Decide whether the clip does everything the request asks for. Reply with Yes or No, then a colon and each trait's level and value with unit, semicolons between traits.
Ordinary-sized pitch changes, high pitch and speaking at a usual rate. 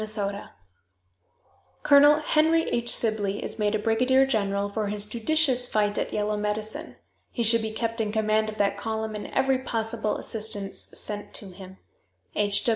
No: narrow, 2.2 semitones; high, 215 Hz; average, 160 wpm